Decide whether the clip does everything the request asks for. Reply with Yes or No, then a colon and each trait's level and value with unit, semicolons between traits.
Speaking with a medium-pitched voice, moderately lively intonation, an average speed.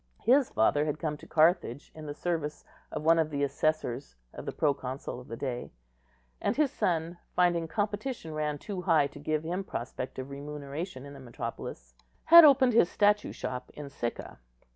Yes: medium, 155 Hz; average, 4.3 semitones; average, 180 wpm